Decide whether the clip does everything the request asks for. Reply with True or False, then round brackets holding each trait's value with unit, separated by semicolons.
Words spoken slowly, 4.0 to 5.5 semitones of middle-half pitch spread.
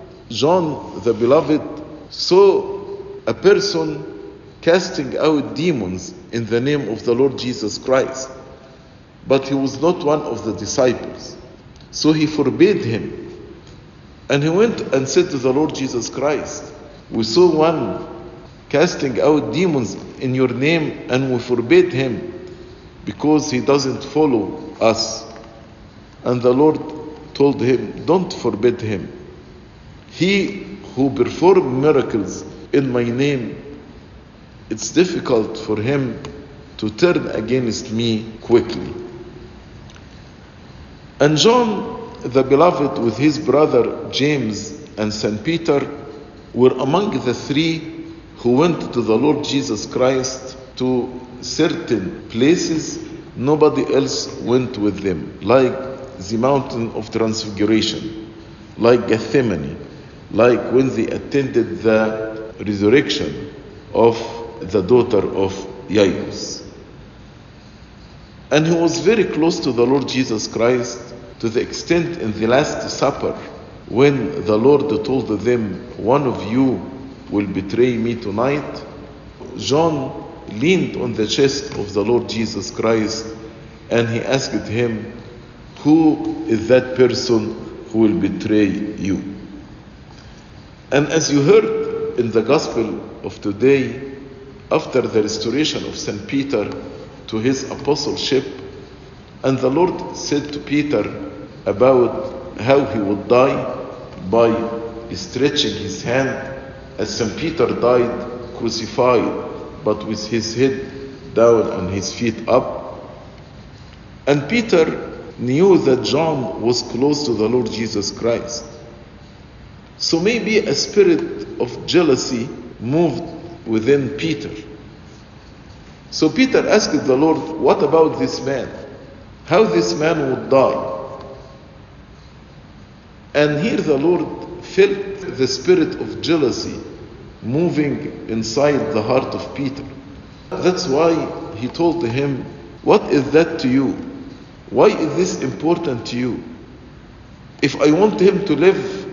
True (120 wpm; 5.1 semitones)